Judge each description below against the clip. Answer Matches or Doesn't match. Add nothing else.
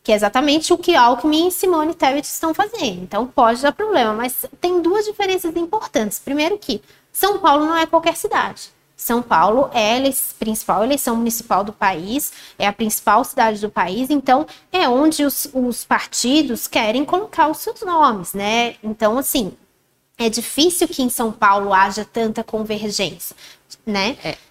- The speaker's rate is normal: Matches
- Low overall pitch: Doesn't match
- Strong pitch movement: Matches